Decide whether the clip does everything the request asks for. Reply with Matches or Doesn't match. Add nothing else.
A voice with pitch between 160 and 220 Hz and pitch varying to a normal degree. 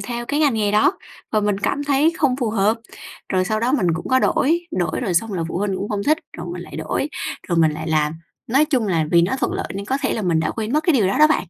Doesn't match